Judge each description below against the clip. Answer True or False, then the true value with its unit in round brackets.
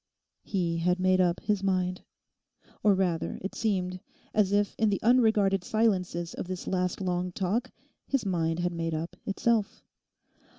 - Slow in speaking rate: False (155 wpm)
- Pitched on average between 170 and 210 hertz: True (185 Hz)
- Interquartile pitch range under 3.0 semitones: True (2.6 semitones)